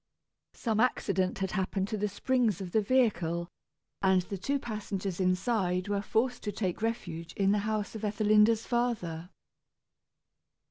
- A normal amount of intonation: Yes, average, 3.1 semitones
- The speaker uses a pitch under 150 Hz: No, high, 205 Hz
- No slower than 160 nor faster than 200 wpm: No, average, 145 wpm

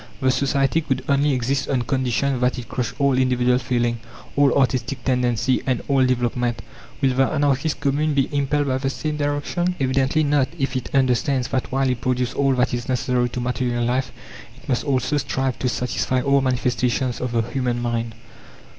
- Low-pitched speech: Yes, low, 130 Hz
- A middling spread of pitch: No, narrow, 1.9 semitones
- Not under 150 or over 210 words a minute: Yes, average, 180 wpm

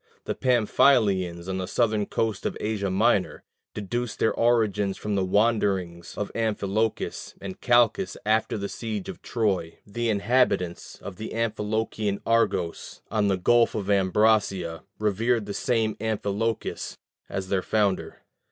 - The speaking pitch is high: No, low, 105 Hz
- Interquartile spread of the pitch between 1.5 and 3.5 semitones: Yes, average, 2.7 semitones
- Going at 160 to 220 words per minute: No, slow, 135 wpm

